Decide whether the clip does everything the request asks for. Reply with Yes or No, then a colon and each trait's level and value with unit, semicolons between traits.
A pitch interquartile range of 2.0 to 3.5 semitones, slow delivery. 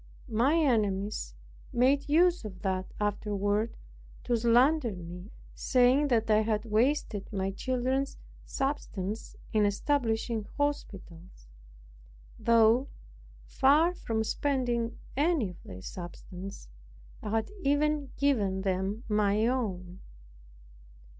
No: average, 5.2 semitones; slow, 100 wpm